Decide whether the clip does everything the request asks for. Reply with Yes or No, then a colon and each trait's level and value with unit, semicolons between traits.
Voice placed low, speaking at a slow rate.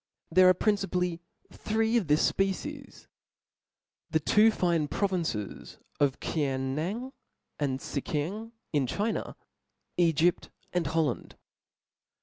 No: medium, 175 Hz; slow, 105 wpm